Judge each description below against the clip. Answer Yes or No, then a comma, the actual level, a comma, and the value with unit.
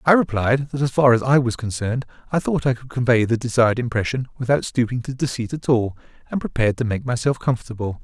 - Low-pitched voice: Yes, low, 125 Hz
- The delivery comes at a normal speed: No, fast, 215 wpm